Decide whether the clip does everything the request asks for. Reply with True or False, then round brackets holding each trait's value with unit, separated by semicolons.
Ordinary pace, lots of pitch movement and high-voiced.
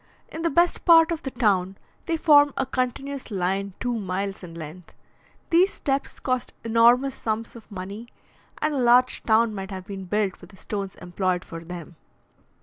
True (175 wpm; 6.0 semitones; 220 Hz)